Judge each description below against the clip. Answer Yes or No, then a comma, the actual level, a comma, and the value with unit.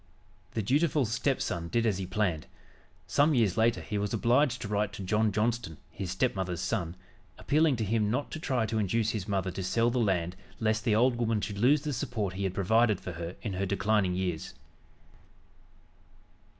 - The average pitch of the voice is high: No, low, 110 Hz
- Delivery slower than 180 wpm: No, average, 190 wpm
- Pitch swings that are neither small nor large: Yes, average, 3.8 semitones